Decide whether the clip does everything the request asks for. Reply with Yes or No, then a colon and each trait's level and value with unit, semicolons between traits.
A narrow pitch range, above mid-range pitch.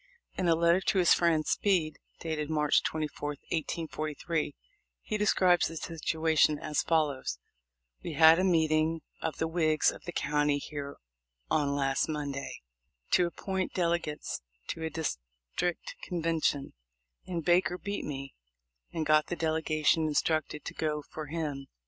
No: narrow, 2.2 semitones; medium, 160 Hz